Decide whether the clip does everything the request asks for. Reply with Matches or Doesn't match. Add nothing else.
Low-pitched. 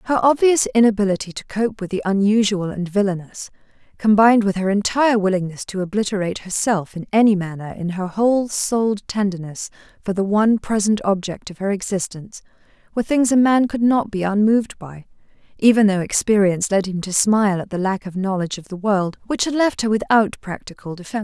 Doesn't match